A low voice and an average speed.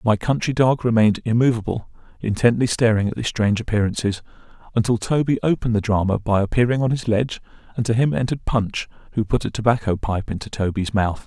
Yes: low, 110 Hz; average, 180 wpm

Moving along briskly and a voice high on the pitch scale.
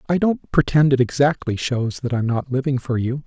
No: fast, 220 wpm; low, 135 Hz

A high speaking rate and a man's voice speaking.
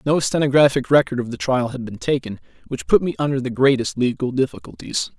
No: average, 195 wpm; male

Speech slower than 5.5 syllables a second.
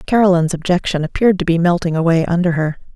No: 7.1 syllables/s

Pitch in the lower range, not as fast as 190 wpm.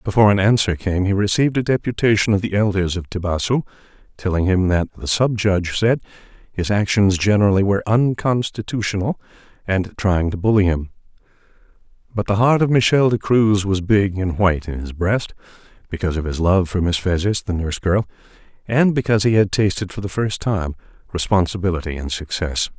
Yes: low, 100 Hz; average, 170 wpm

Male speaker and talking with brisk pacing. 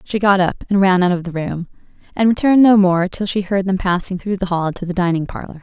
No: female; fast, 265 wpm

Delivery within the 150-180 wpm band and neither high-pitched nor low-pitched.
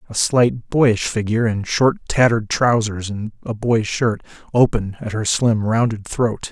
No: average, 165 wpm; low, 115 Hz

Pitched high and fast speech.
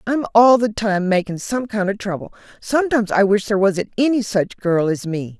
Yes: high, 205 Hz; fast, 210 wpm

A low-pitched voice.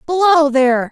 No: very high, 290 Hz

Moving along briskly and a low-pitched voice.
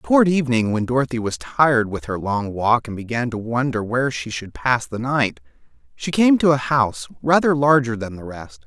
Yes: fast, 210 wpm; low, 125 Hz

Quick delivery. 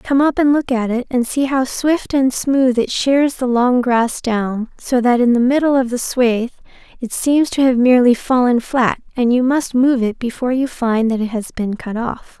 Yes: fast, 225 wpm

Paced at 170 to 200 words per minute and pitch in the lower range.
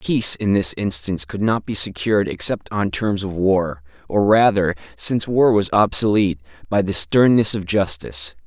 No: average, 155 wpm; very low, 95 Hz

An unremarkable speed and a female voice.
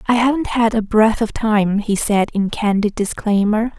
Yes: average, 190 wpm; female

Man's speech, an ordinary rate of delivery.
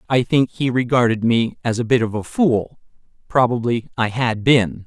Yes: male; average, 185 wpm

